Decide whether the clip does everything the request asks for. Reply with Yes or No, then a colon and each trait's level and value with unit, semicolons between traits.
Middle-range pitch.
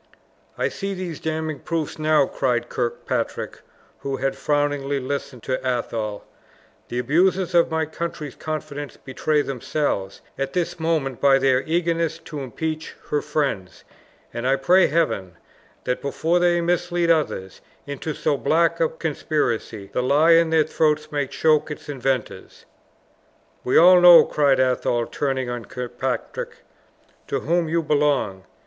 Yes: medium, 145 Hz